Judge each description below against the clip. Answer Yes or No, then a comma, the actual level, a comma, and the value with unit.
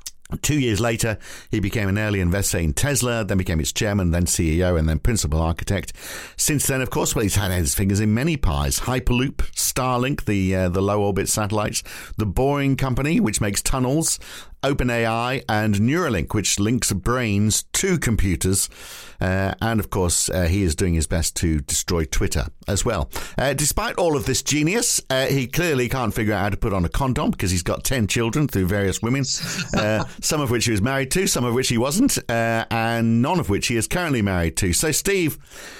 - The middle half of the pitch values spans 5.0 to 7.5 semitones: Yes, wide, 5.6 semitones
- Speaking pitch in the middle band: No, low, 110 Hz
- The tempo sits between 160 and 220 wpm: Yes, average, 200 wpm